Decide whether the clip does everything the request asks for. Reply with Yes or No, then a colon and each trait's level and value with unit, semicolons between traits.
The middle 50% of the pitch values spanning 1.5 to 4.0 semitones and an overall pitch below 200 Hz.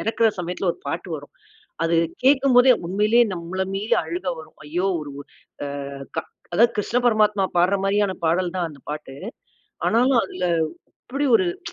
No: average, 4.9 semitones; high, 190 Hz